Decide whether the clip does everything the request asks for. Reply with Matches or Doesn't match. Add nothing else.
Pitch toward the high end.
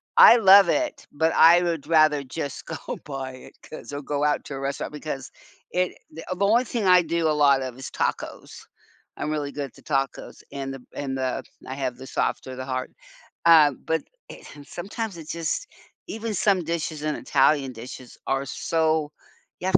Doesn't match